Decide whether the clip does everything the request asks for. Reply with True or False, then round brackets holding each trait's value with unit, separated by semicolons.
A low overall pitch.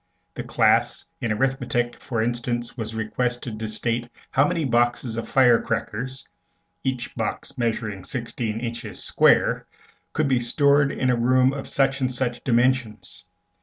True (120 Hz)